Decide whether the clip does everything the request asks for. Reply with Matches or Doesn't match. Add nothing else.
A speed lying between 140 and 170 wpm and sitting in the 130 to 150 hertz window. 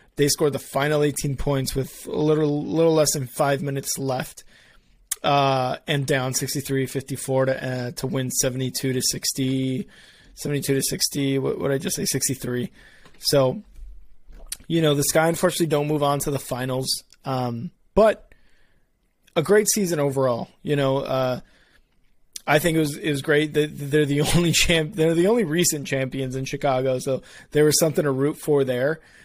Matches